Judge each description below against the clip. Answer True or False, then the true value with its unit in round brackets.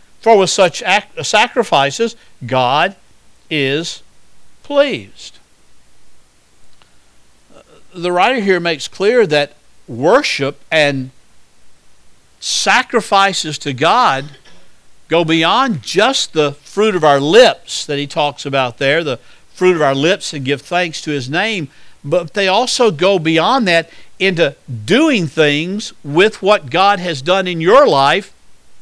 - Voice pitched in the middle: True (170 Hz)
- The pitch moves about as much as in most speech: False (5.8 semitones)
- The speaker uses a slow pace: True (125 wpm)